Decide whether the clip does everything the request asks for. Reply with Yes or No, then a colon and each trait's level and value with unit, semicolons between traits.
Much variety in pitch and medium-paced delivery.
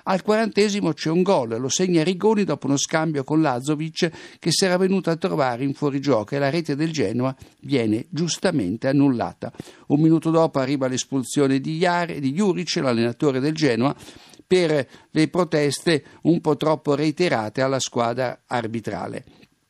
No: average, 4.1 semitones; average, 155 wpm